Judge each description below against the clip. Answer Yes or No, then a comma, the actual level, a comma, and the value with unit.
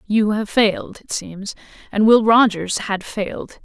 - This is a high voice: Yes, high, 210 Hz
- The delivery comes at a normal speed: Yes, average, 165 wpm